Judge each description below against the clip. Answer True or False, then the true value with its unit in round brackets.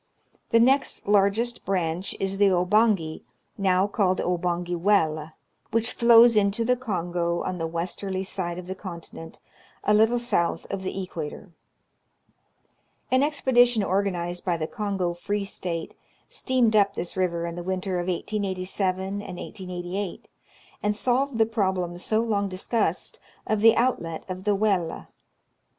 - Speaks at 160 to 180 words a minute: False (145 wpm)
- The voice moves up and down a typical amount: True (3.4 semitones)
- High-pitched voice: True (195 Hz)